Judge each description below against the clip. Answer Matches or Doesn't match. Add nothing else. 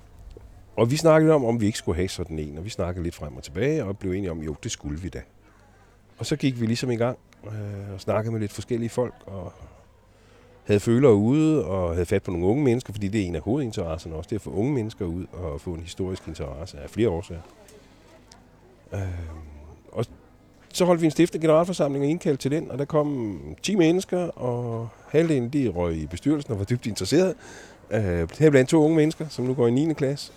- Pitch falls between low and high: Doesn't match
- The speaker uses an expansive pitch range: Matches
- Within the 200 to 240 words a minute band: Matches